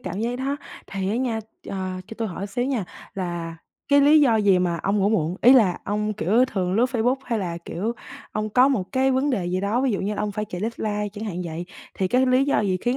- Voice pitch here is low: No, high, 210 Hz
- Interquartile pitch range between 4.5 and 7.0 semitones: Yes, average, 4.8 semitones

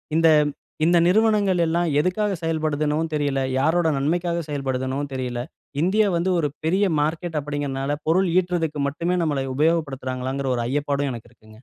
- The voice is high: No, medium, 155 Hz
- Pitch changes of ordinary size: Yes, average, 4.1 semitones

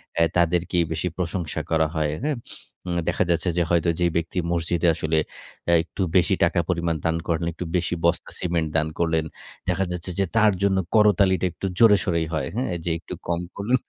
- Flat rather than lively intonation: Yes, narrow, 2.1 semitones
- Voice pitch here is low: Yes, very low, 85 Hz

